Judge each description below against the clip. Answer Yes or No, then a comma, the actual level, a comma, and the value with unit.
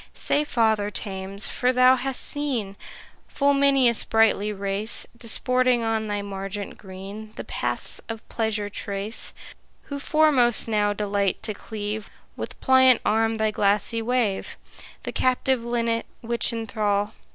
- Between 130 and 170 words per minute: Yes, slow, 135 wpm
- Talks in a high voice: Yes, high, 225 Hz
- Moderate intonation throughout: Yes, average, 3.3 semitones